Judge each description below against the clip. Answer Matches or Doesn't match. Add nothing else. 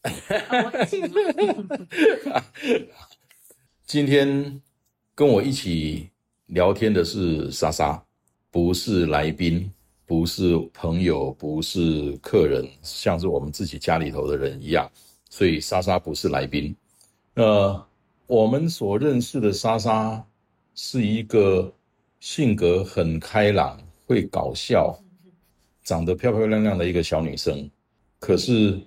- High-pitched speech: Doesn't match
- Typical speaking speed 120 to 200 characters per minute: Matches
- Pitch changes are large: Matches